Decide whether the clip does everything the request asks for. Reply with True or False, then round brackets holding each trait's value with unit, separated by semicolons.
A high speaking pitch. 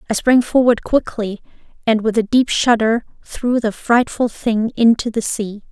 True (230 Hz)